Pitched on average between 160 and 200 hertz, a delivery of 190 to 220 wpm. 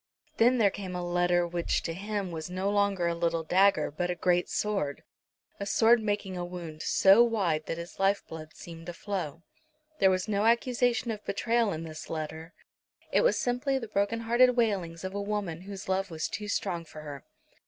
Yes: high, 190 Hz; average, 195 wpm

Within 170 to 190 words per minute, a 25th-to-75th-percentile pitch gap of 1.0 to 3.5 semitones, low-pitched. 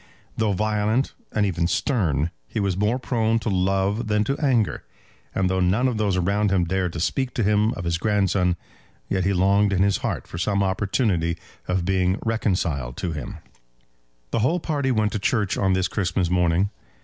Yes: average, 185 wpm; average, 3.0 semitones; low, 100 Hz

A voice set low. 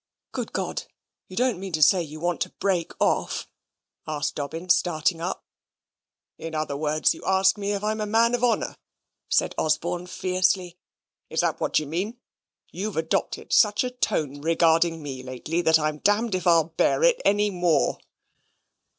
No: medium, 175 Hz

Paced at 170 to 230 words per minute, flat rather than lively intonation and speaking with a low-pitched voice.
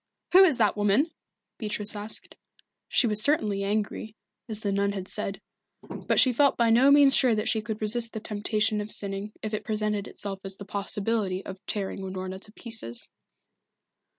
No: average, 180 wpm; narrow, 2.1 semitones; high, 210 Hz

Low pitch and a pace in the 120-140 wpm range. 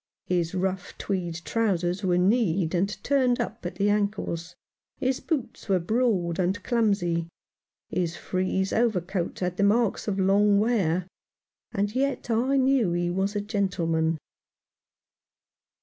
No: high, 195 Hz; slow, 135 wpm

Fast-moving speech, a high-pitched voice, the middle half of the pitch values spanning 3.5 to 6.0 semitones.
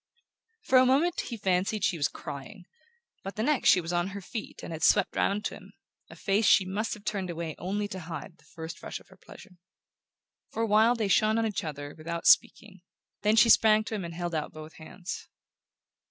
Yes: fast, 215 wpm; high, 195 Hz; average, 4.2 semitones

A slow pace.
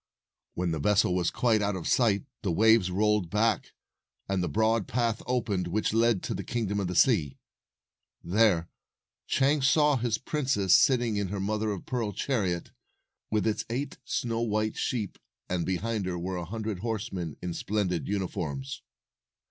No: average, 165 wpm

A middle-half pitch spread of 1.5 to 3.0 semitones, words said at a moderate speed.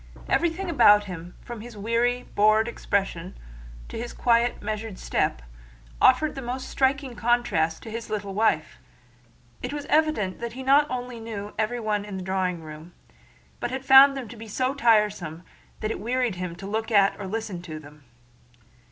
No: average, 4.2 semitones; average, 175 wpm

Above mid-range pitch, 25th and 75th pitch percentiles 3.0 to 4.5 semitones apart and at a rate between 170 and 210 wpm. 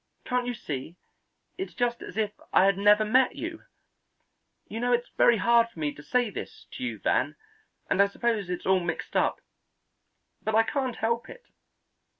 Yes: high, 225 Hz; average, 3.7 semitones; average, 180 wpm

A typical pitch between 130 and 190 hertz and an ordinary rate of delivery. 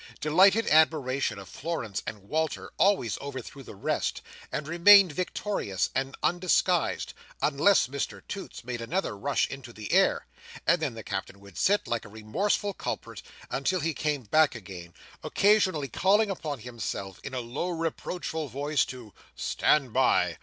Yes: medium, 140 Hz; average, 150 wpm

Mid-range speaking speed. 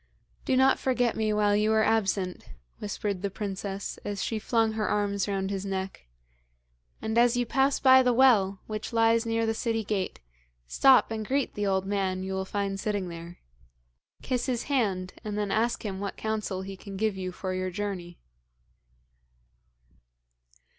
Yes: average, 170 wpm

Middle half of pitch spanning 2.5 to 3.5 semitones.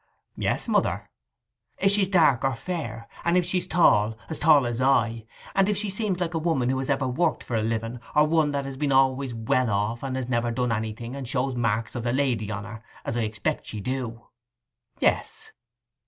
No: average, 4.8 semitones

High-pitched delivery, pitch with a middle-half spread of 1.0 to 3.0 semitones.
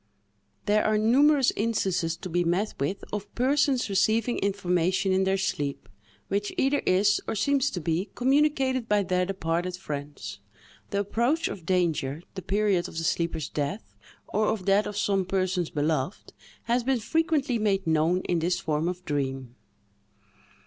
No: high, 195 Hz; average, 4.5 semitones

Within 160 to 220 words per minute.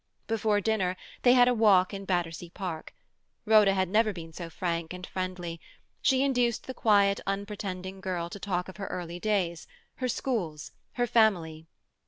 Yes: average, 165 wpm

